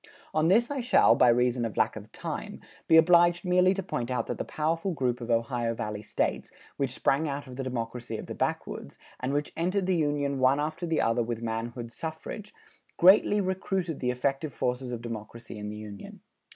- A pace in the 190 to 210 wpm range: Yes, average, 200 wpm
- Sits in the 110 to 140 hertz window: Yes, low, 135 Hz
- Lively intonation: Yes, wide, 6.0 semitones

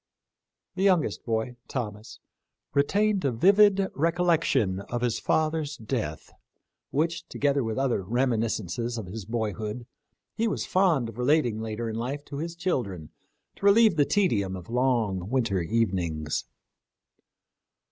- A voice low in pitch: Yes, low, 125 Hz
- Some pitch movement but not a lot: No, wide, 6.6 semitones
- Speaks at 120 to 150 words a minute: Yes, slow, 135 wpm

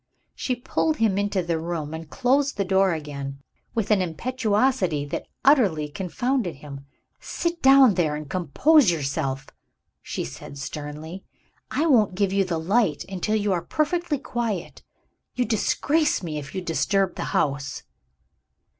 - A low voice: No, high, 190 Hz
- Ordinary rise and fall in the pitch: No, wide, 7.9 semitones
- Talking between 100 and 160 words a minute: Yes, average, 145 wpm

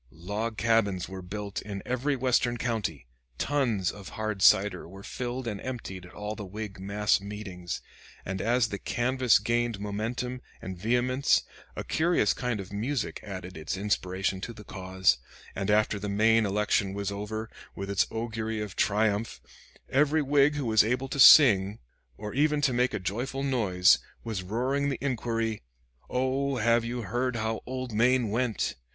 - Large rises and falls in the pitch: No, average, 3.8 semitones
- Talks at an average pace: Yes, average, 165 wpm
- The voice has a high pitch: No, low, 110 Hz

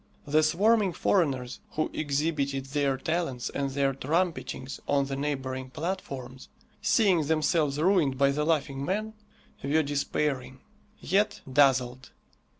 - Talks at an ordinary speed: No, slow, 120 wpm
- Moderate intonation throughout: Yes, average, 3.4 semitones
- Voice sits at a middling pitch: Yes, medium, 145 Hz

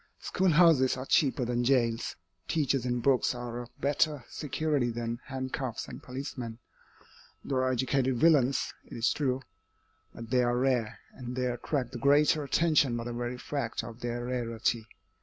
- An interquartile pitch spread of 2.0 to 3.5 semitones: Yes, narrow, 2.5 semitones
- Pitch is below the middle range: Yes, low, 125 Hz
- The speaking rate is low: No, average, 160 wpm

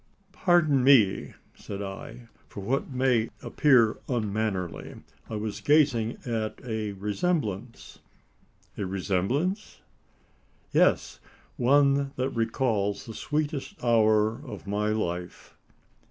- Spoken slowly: Yes, slow, 100 wpm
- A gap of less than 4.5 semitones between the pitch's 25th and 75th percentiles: No, average, 4.8 semitones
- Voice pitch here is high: No, low, 115 Hz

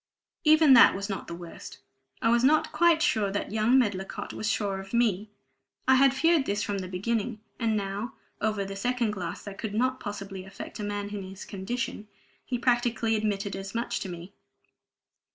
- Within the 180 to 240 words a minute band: Yes, average, 190 wpm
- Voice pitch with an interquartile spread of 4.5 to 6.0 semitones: No, average, 3.5 semitones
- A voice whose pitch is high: Yes, high, 210 Hz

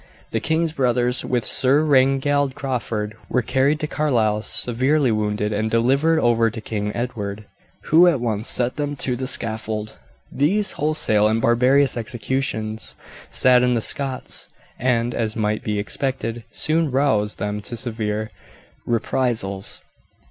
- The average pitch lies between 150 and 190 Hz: No, low, 120 Hz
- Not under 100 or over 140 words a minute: Yes, slow, 135 wpm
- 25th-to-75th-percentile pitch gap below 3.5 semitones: No, average, 3.9 semitones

